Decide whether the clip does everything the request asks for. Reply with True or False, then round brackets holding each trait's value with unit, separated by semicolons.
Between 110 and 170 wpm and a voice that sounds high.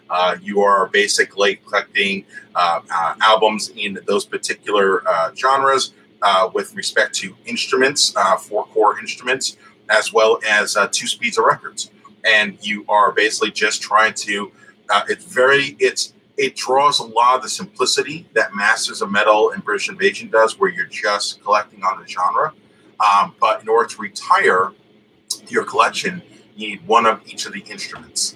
True (165 wpm; 235 Hz)